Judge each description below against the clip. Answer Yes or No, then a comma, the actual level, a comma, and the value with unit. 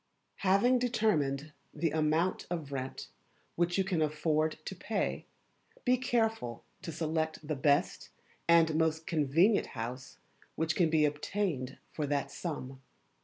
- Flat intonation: No, average, 3.3 semitones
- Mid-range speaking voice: Yes, medium, 160 Hz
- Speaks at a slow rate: Yes, slow, 130 wpm